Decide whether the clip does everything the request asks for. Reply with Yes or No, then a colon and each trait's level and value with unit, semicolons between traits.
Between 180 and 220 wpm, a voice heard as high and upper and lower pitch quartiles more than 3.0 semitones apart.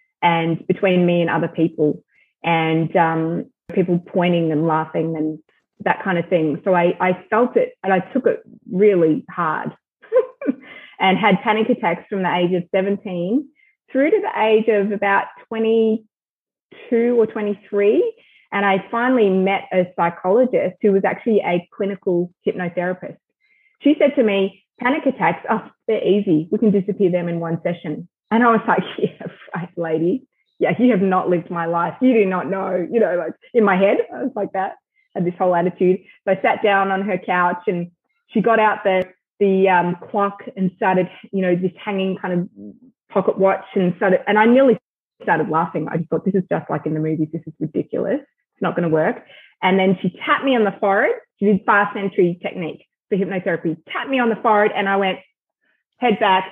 Yes: average, 195 wpm; high, 195 Hz; average, 4.1 semitones